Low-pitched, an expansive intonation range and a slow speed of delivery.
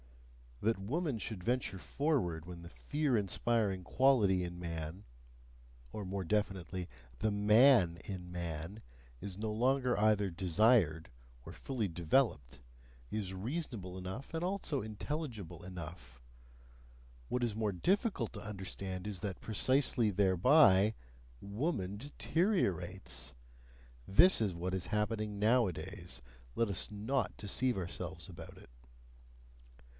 No: low, 100 Hz; average, 5.0 semitones; slow, 120 wpm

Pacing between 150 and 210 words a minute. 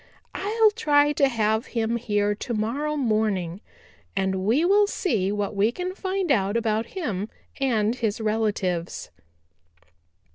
No: slow, 135 wpm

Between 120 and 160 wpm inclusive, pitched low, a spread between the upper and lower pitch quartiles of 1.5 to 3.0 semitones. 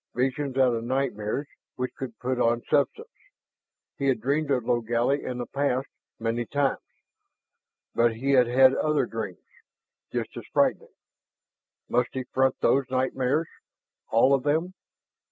Yes: average, 140 wpm; low, 130 Hz; narrow, 2.5 semitones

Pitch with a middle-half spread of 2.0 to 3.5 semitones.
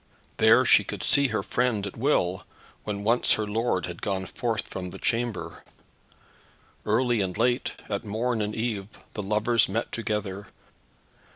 Yes: average, 3.1 semitones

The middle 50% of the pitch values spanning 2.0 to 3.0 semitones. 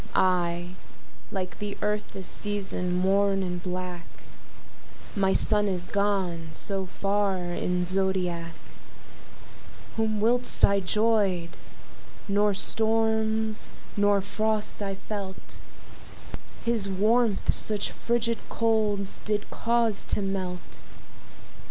Yes: narrow, 2.6 semitones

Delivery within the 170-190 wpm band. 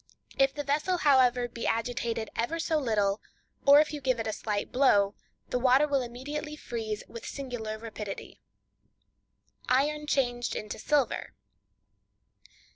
No: slow, 135 wpm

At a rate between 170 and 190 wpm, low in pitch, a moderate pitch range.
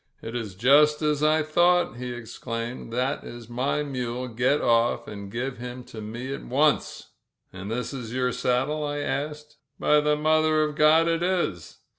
Yes: average, 180 wpm; low, 130 Hz; average, 4.0 semitones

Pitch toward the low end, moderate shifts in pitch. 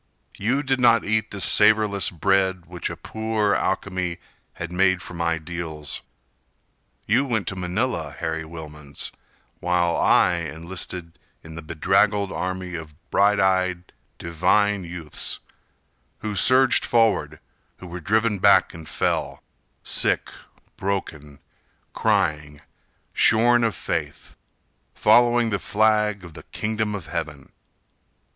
Yes: very low, 95 Hz; average, 4.2 semitones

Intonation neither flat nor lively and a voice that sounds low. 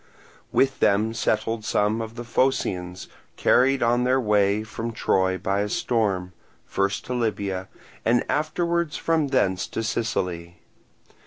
Yes: average, 4.1 semitones; low, 110 Hz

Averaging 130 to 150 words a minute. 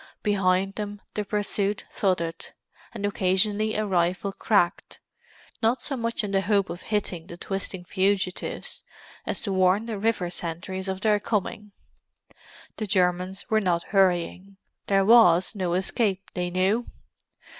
Yes: average, 140 wpm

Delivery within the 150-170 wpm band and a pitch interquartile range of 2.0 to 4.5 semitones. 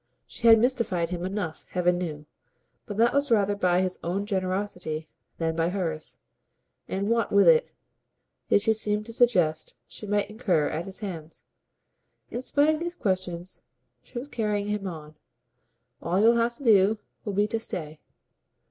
Yes: average, 165 wpm; average, 4.2 semitones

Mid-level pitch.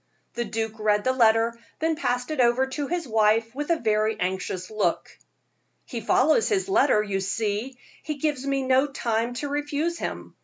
No: high, 245 Hz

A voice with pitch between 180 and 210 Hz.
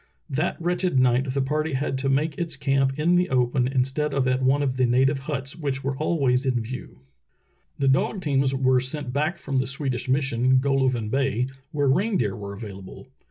No: low, 135 Hz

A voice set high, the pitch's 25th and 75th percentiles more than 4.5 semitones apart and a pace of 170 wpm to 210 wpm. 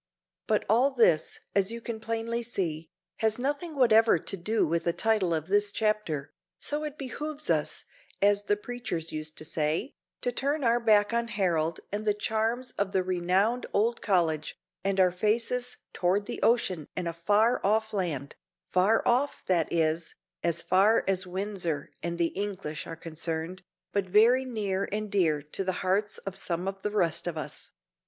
Yes: high, 200 Hz; average, 4.9 semitones; average, 175 wpm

